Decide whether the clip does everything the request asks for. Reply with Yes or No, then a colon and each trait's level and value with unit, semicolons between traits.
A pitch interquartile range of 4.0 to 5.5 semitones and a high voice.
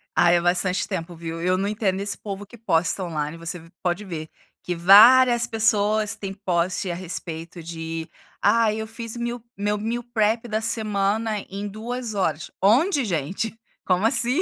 Yes: average, 4.3 semitones; high, 200 Hz